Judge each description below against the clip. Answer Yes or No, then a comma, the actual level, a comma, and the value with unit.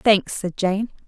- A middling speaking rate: Yes, average, 165 wpm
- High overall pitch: Yes, high, 200 Hz